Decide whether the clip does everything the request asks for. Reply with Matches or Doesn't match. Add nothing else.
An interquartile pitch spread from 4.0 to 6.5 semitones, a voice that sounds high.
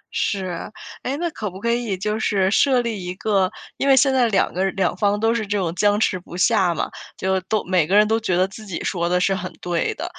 Doesn't match